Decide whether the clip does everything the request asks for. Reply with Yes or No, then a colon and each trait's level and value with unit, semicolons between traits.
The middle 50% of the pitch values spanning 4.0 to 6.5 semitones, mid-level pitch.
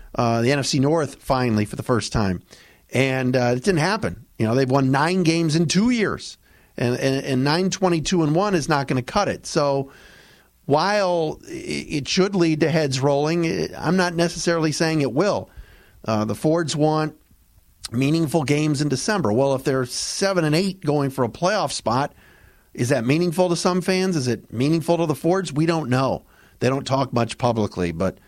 Yes: average, 4.7 semitones; medium, 150 Hz